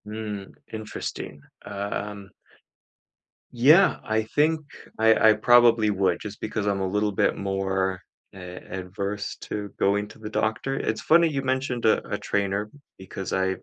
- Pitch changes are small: Yes, narrow, 2.3 semitones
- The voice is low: Yes, low, 105 Hz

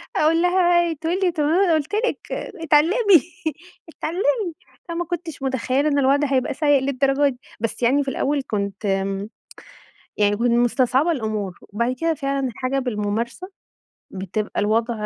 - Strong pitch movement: Yes, wide, 5.8 semitones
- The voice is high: Yes, very high, 275 Hz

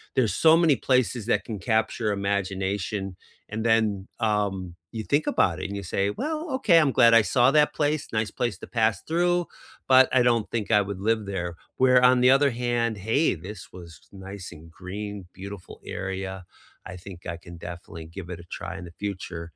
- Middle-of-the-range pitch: No, low, 105 Hz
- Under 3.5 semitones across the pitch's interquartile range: No, average, 4.5 semitones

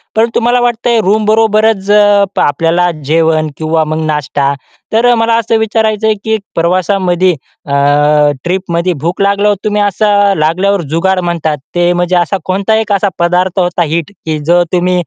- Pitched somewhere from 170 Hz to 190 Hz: Yes, medium, 185 Hz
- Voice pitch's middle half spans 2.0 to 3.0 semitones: No, average, 3.8 semitones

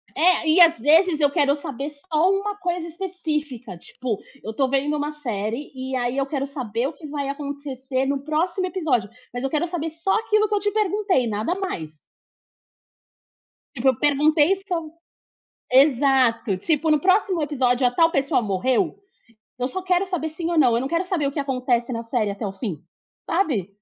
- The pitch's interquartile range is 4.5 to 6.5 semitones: Yes, average, 5.0 semitones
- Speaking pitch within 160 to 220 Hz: No, very high, 285 Hz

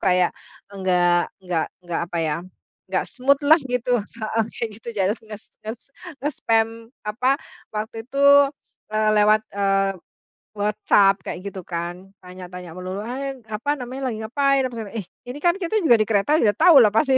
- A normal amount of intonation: Yes, average, 4.6 semitones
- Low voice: No, high, 215 Hz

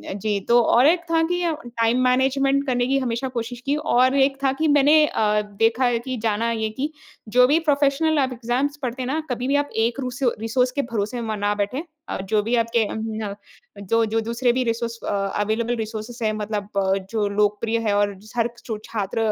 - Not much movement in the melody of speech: No, average, 3.3 semitones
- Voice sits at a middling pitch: No, high, 235 Hz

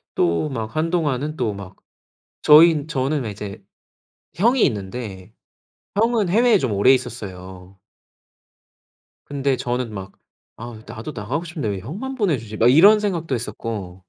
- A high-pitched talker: No, low, 125 Hz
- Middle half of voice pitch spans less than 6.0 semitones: No, wide, 7.7 semitones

